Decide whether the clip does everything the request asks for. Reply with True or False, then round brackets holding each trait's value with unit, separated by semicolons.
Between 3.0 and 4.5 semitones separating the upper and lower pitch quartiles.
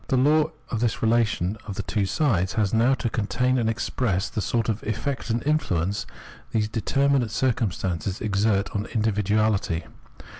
True (3.4 semitones)